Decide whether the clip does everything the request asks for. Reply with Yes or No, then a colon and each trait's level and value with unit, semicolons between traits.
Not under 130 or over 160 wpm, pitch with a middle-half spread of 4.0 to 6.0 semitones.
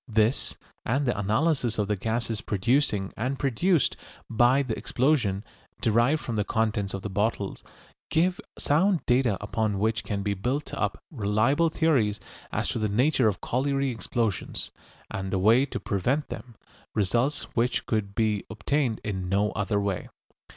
Yes: average, 155 wpm; average, 4.6 semitones